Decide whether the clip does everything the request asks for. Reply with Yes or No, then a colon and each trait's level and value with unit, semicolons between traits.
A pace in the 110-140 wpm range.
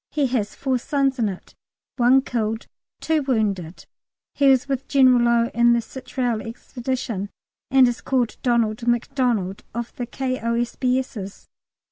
Yes: slow, 135 wpm